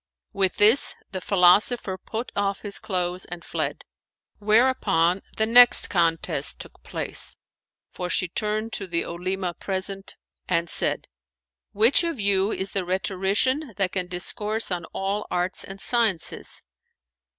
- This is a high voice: Yes, high, 195 Hz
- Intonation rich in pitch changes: No, average, 2.9 semitones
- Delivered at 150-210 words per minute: No, average, 140 wpm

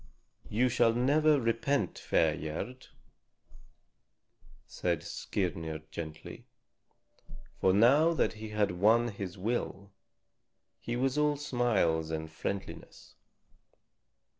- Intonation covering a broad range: Yes, wide, 6.3 semitones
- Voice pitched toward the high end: No, low, 110 Hz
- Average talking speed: No, slow, 95 wpm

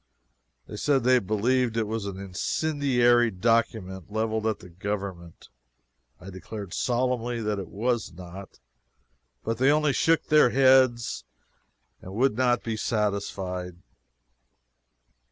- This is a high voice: No, low, 110 Hz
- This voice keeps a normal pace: No, slow, 120 wpm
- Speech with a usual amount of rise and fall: Yes, average, 4.1 semitones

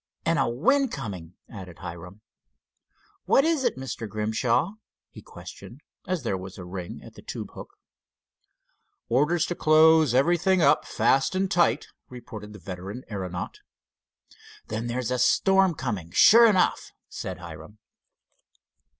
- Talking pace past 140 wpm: No, slow, 135 wpm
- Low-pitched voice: Yes, low, 125 Hz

